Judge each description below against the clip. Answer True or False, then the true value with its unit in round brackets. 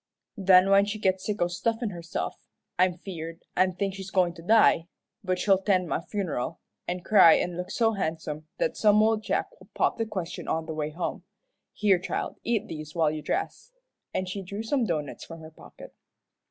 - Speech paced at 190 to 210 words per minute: True (195 wpm)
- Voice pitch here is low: False (185 Hz)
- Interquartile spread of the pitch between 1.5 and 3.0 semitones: False (3.8 semitones)